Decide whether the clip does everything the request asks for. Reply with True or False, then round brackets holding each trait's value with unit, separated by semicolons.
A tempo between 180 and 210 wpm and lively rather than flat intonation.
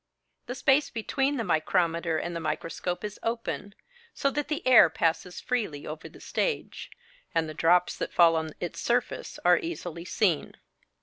False (165 wpm; 6.9 semitones)